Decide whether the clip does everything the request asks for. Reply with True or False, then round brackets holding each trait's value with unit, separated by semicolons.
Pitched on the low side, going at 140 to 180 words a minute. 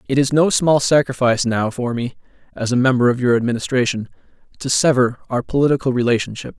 True (125 Hz; 175 wpm)